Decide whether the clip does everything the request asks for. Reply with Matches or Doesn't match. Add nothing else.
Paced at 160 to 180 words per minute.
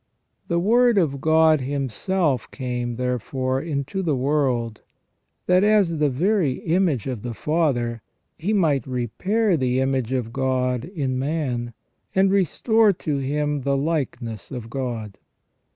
Doesn't match